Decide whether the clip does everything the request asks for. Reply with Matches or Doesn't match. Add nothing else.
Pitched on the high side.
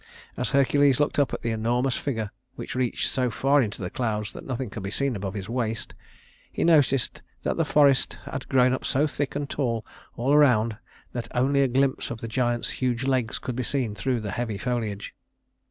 Doesn't match